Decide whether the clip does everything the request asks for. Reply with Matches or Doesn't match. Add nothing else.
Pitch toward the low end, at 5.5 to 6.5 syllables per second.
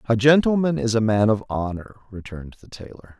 Matches